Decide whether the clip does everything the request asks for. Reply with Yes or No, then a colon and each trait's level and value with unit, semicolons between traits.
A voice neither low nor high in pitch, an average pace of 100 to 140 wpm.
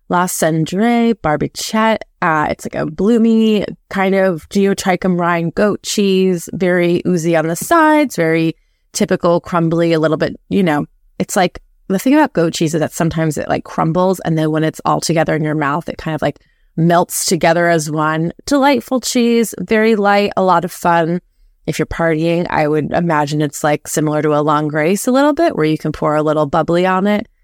No: medium, 170 Hz; average, 195 wpm